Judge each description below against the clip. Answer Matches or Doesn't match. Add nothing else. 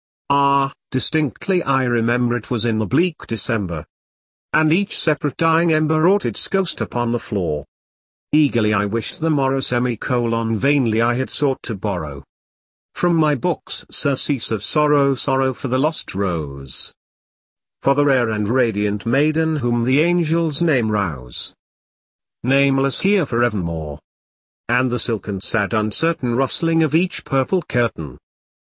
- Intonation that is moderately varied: Doesn't match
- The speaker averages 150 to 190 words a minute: Doesn't match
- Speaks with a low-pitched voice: Matches